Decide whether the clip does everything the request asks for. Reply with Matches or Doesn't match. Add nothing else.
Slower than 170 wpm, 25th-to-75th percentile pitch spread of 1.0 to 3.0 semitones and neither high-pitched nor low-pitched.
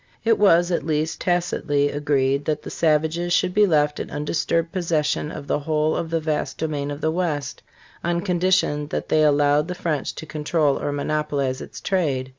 Doesn't match